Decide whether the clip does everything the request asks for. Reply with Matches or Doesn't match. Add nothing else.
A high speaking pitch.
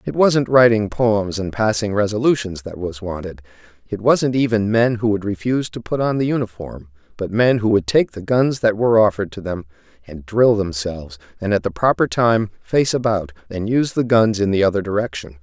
Doesn't match